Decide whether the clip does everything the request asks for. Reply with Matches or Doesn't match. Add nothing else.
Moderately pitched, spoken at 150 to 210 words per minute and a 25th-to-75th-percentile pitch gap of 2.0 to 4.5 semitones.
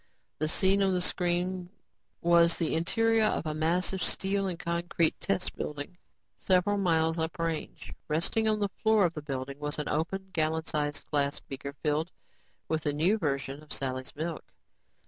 Matches